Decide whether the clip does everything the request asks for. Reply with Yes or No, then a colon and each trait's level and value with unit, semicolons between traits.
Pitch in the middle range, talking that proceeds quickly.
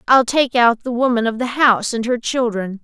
No: high, 240 Hz; fast, 230 wpm